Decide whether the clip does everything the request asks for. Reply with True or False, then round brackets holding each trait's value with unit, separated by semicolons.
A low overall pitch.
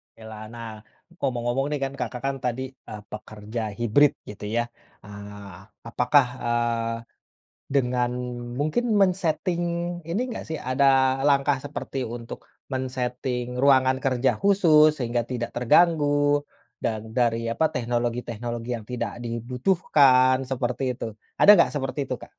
True (125 Hz)